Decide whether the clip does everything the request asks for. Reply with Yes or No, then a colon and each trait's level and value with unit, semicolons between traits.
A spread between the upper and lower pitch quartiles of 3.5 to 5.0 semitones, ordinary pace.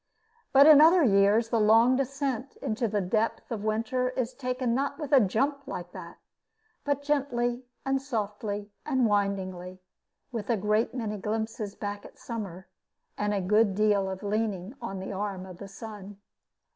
Yes: average, 4.0 semitones; average, 170 wpm